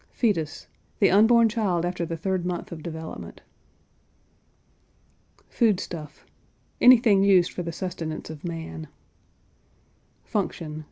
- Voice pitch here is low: No, medium, 175 Hz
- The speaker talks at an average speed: No, slow, 110 wpm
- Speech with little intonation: No, average, 3.7 semitones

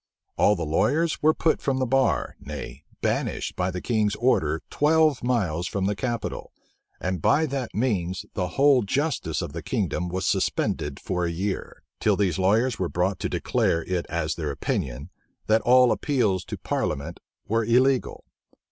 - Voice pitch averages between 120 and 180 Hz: No, low, 100 Hz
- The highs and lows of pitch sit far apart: Yes, wide, 6.6 semitones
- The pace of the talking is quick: No, average, 165 wpm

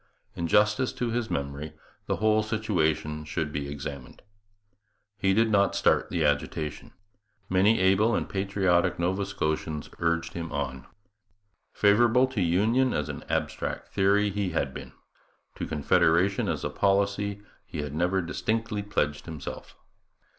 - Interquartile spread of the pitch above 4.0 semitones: Yes, average, 5.0 semitones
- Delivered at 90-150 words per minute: Yes, average, 140 wpm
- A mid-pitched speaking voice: No, very low, 95 Hz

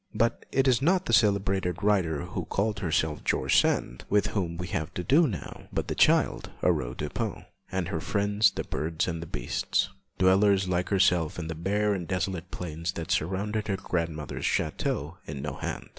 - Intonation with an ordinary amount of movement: Yes, average, 3.9 semitones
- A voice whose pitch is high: No, very low, 90 Hz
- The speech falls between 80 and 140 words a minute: No, average, 175 wpm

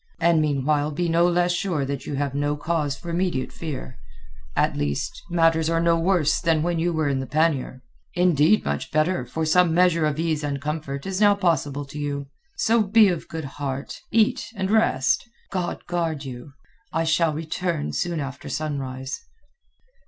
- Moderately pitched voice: Yes, medium, 160 Hz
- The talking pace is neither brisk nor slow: Yes, average, 175 wpm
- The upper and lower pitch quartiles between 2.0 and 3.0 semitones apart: No, average, 3.5 semitones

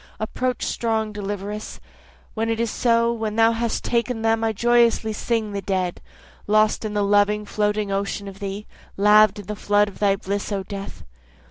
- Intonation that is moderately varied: No, narrow, 1.9 semitones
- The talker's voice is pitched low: No, high, 210 Hz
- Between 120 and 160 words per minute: No, average, 175 wpm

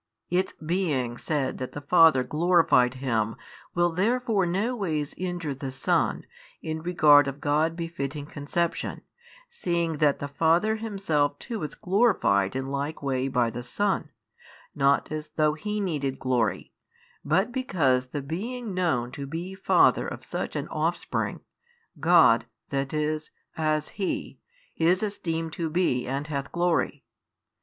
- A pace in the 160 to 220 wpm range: No, average, 140 wpm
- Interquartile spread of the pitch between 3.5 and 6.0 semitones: Yes, average, 4.5 semitones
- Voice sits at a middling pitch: Yes, medium, 155 Hz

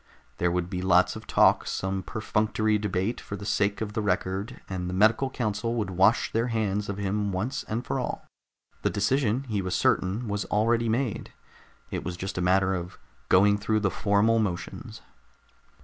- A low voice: Yes, low, 105 Hz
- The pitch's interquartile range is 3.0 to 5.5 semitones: No, narrow, 2.6 semitones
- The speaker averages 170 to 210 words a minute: Yes, average, 180 wpm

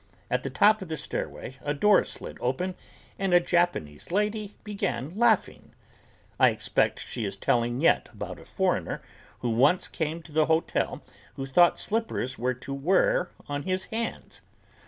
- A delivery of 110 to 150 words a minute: No, average, 160 wpm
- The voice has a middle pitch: Yes, medium, 160 Hz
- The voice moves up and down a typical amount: No, wide, 6.6 semitones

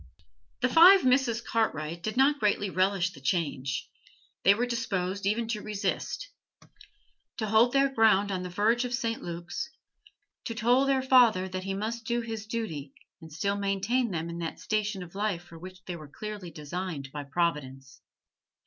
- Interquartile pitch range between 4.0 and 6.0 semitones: Yes, average, 5.1 semitones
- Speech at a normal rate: Yes, average, 170 wpm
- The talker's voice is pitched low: No, high, 200 Hz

